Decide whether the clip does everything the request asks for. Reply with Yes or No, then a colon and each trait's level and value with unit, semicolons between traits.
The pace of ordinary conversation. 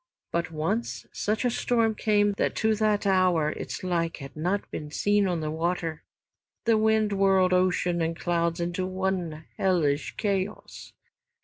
Yes: average, 145 wpm